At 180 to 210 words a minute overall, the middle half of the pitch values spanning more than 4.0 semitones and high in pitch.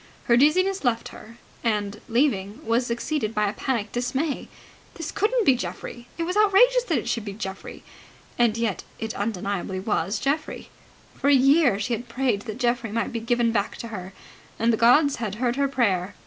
Yes: average, 190 wpm; average, 4.6 semitones; high, 235 Hz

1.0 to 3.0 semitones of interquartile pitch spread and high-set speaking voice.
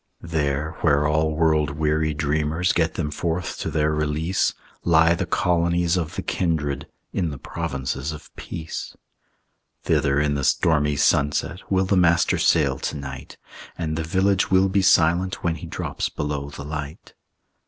No: narrow, 2.6 semitones; very low, 80 Hz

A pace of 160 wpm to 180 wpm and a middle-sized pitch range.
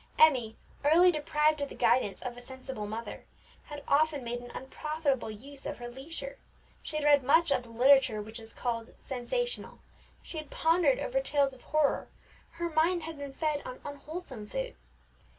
Yes: average, 175 wpm; average, 4.4 semitones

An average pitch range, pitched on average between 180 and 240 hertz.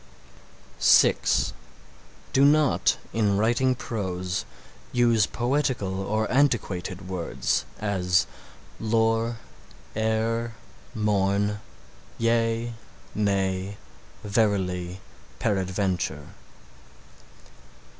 No: average, 3.4 semitones; low, 105 Hz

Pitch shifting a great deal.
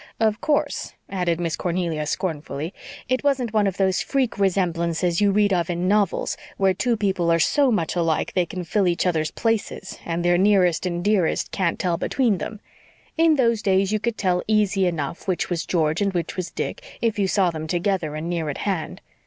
No: average, 3.5 semitones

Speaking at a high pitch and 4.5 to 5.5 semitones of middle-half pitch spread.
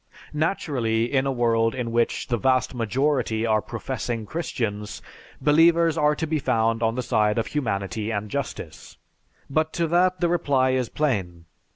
No: low, 125 Hz; average, 4.9 semitones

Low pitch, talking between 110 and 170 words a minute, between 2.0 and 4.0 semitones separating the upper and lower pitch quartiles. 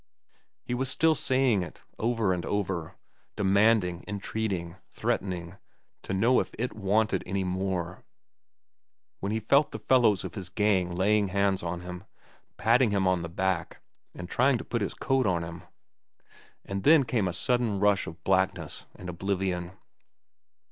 Yes: very low, 95 Hz; average, 150 wpm; average, 3.6 semitones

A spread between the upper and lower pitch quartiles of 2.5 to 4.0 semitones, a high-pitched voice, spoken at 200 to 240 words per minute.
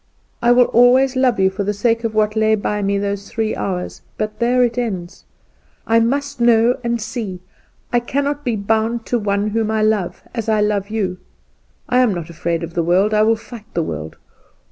Yes: average, 3.0 semitones; high, 220 Hz; fast, 205 wpm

